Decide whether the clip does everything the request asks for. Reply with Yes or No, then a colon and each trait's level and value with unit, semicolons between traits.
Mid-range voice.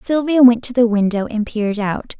No: high, 230 Hz